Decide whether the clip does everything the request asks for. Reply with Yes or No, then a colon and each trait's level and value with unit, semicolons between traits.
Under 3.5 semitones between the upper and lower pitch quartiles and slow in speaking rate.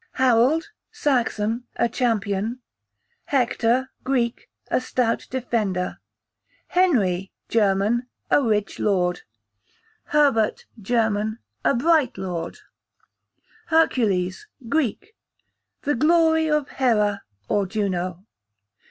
No: average, 5.0 semitones; slow, 85 wpm